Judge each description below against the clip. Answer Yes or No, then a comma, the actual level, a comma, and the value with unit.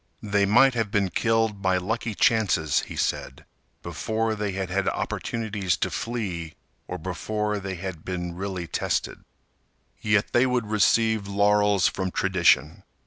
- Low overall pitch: Yes, low, 100 Hz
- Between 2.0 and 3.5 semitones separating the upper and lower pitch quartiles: Yes, average, 3.0 semitones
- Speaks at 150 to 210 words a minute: No, average, 140 wpm